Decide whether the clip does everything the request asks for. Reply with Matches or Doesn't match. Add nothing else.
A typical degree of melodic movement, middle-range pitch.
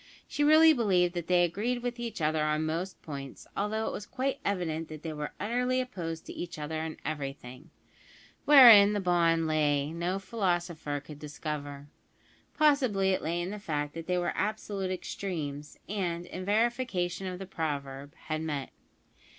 Matches